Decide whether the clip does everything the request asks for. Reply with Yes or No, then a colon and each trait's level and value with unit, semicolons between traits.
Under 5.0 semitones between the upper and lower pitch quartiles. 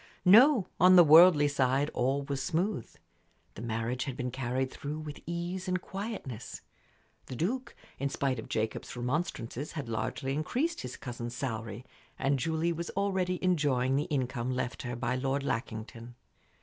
No: wide, 5.6 semitones